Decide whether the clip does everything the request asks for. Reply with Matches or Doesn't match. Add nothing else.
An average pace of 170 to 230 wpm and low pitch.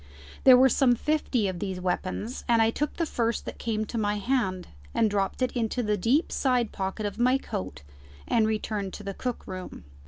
Doesn't match